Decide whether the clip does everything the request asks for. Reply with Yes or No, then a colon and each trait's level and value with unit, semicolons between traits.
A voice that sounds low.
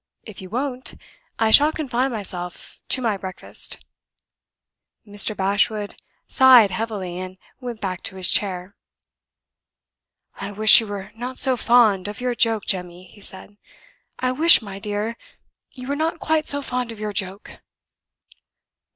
No: high, 215 Hz